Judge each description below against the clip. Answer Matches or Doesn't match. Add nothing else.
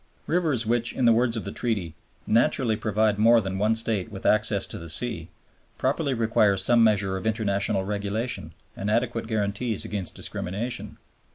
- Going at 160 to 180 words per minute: Matches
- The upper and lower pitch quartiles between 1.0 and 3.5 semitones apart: Matches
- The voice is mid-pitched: Doesn't match